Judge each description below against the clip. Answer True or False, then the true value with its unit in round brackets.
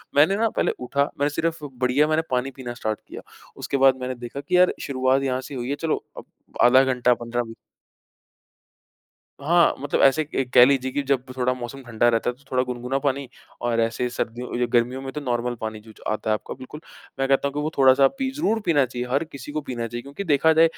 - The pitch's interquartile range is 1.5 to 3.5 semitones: True (2.7 semitones)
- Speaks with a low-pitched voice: True (130 Hz)